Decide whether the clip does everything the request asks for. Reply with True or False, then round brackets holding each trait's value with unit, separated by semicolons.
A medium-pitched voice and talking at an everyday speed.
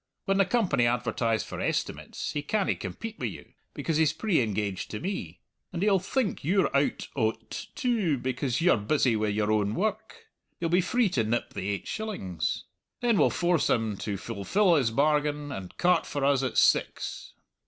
True (145 Hz; 180 wpm)